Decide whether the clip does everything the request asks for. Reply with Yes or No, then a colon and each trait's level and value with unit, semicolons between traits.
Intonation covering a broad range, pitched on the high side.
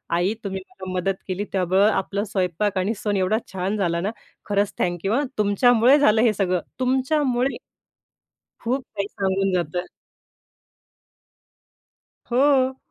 No: average, 4.2 semitones; high, 200 Hz